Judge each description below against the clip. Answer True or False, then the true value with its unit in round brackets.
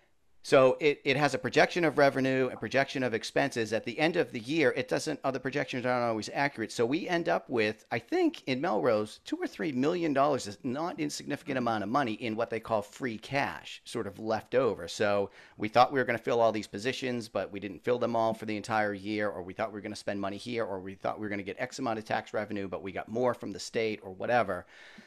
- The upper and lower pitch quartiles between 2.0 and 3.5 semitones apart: False (4.3 semitones)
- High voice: False (115 Hz)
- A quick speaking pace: True (250 wpm)